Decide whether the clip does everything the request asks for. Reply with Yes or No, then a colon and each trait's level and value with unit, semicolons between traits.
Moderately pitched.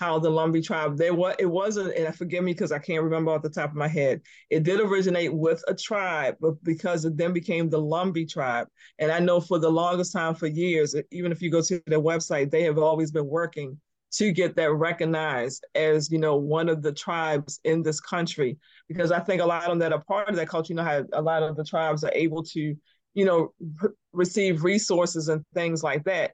Yes: medium, 165 Hz